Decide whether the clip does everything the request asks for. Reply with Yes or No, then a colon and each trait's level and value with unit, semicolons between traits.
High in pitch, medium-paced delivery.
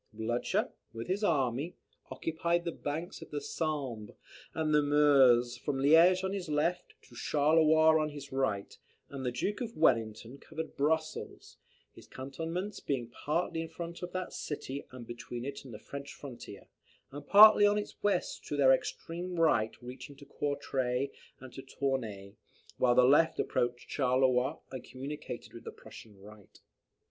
No: medium, 140 Hz; average, 155 wpm